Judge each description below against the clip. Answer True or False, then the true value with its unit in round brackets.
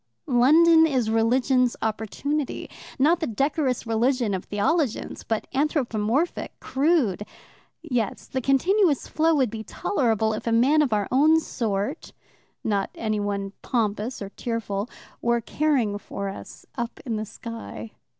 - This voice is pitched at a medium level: False (240 Hz)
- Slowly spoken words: True (130 wpm)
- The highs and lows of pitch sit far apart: False (4.9 semitones)